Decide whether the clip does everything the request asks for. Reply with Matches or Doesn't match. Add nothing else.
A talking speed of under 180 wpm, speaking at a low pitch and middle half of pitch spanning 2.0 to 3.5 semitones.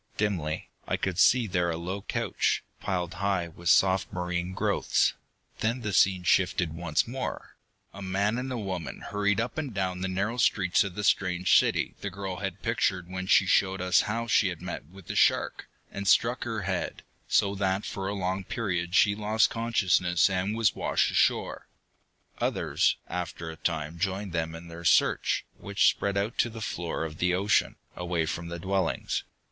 Doesn't match